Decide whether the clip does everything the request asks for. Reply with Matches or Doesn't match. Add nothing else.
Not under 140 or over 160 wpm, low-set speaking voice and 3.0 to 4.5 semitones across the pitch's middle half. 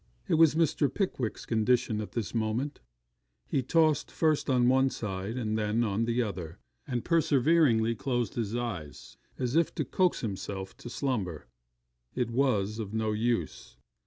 Matches